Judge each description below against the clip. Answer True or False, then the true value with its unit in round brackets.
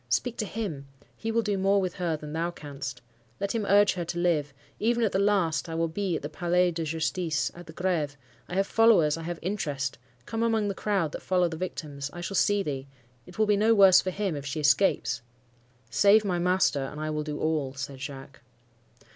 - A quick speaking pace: True (215 wpm)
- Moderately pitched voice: True (175 Hz)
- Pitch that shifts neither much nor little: True (4.9 semitones)